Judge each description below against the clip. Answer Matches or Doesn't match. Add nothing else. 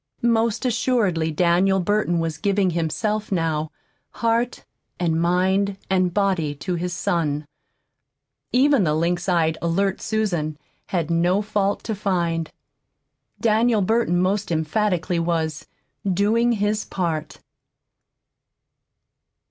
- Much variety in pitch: Doesn't match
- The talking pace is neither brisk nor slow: Doesn't match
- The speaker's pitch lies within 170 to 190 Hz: Matches